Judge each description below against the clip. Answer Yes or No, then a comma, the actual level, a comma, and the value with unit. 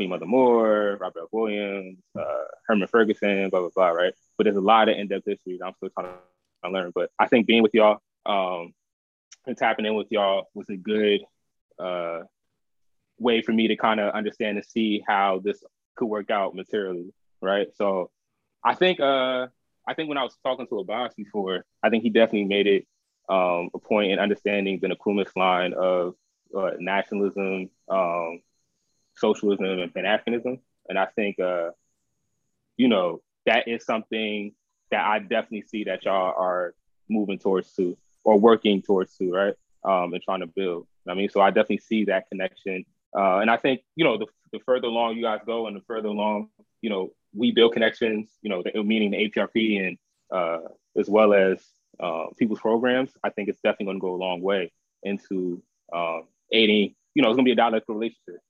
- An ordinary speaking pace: Yes, average, 195 wpm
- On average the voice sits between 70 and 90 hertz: No, low, 100 Hz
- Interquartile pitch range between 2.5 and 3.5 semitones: Yes, average, 3.0 semitones